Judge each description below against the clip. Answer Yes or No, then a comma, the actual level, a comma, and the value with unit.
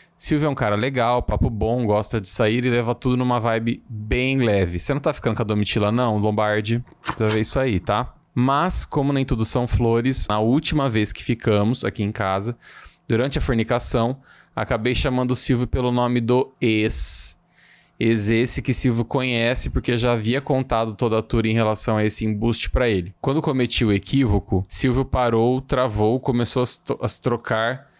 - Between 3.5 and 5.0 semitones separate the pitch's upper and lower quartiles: No, average, 3.0 semitones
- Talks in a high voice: No, low, 120 Hz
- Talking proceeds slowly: No, fast, 185 wpm